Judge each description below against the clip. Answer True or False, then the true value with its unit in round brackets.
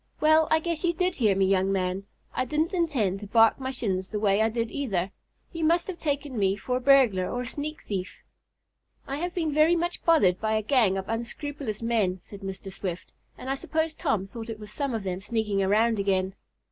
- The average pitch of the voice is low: False (225 Hz)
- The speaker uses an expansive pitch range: True (7.0 semitones)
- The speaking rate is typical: False (220 wpm)